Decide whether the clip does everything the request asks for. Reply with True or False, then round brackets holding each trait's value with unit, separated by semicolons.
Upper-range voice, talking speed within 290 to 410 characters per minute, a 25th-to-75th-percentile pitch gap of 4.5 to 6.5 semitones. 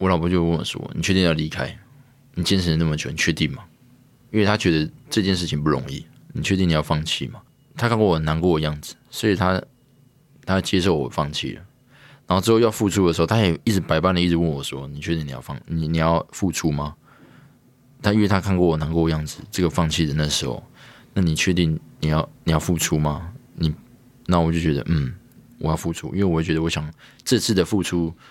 False (85 Hz; 320 characters per minute; 5.4 semitones)